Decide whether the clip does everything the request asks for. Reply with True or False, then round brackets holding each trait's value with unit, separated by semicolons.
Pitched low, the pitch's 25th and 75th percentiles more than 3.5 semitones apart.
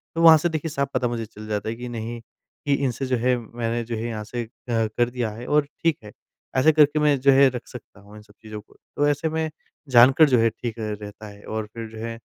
True (120 Hz; 4.0 semitones)